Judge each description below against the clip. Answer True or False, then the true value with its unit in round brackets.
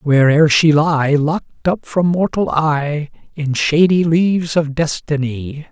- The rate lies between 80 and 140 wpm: True (135 wpm)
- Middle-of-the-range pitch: True (155 Hz)